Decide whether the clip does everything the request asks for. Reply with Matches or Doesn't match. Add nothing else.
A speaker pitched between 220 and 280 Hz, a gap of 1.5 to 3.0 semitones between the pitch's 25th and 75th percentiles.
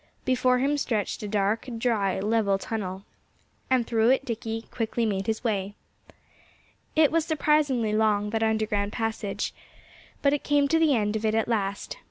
Doesn't match